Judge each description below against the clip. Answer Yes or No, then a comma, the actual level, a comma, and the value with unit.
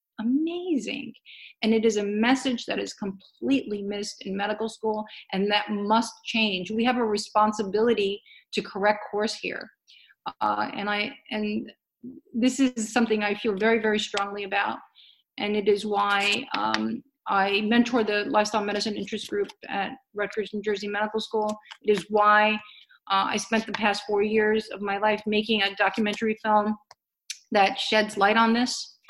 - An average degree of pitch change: No, narrow, 1.8 semitones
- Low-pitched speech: No, high, 215 Hz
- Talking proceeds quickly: No, average, 160 wpm